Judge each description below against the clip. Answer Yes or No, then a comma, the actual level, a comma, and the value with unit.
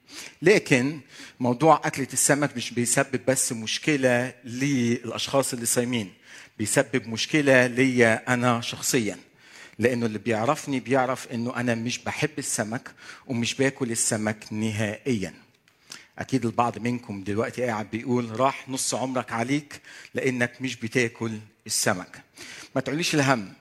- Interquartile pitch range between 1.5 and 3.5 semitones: Yes, narrow, 2.6 semitones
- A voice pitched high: No, low, 125 Hz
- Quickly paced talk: No, average, 115 wpm